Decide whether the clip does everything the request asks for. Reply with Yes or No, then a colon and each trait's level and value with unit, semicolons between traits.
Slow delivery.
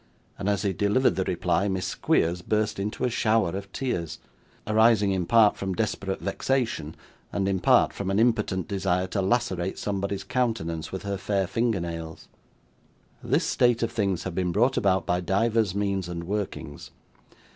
No: average, 165 wpm